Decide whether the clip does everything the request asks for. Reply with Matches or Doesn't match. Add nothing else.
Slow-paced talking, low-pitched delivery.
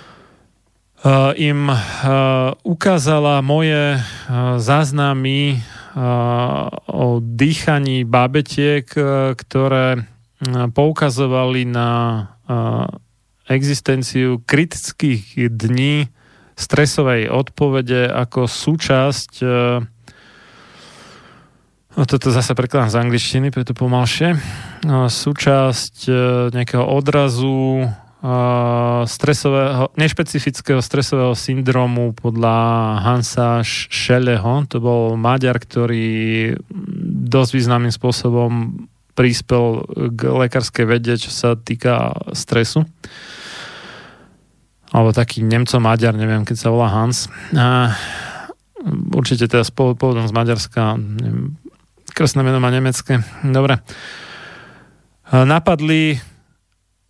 Matches